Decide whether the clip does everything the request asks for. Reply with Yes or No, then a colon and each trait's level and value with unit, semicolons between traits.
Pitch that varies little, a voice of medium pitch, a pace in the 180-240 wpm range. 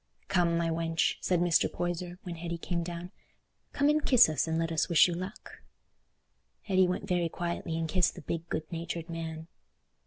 Yes: narrow, 1.4 semitones; medium, 170 Hz; average, 185 wpm